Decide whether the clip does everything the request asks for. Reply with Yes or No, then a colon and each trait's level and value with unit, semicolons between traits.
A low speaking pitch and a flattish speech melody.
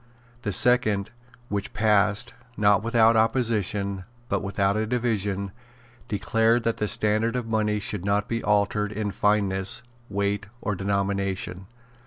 Yes: low, 105 Hz; narrow, 2.0 semitones